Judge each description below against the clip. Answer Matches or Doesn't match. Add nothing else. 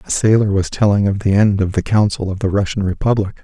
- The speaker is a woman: Doesn't match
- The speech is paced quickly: Matches